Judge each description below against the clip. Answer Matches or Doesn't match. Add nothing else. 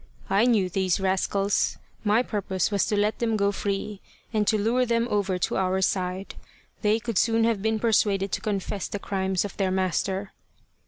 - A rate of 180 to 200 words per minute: Matches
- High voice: Matches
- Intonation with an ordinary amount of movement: Doesn't match